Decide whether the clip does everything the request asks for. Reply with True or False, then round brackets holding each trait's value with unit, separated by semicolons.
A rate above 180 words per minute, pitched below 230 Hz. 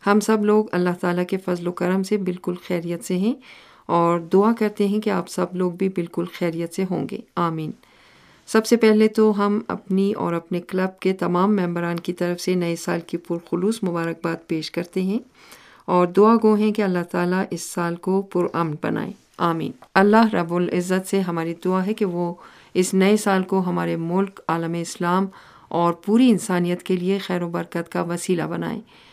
True (190 wpm; 185 Hz)